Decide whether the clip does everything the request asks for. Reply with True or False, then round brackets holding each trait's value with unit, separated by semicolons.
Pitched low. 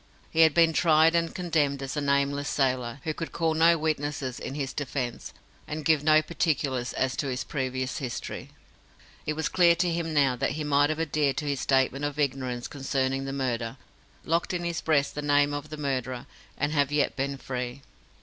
False (145 Hz)